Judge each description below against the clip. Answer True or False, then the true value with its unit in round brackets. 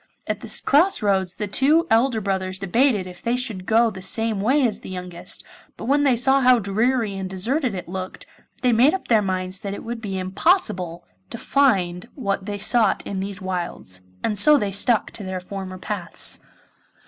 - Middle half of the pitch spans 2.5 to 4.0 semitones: False (4.7 semitones)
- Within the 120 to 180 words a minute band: False (195 wpm)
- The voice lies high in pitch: True (205 Hz)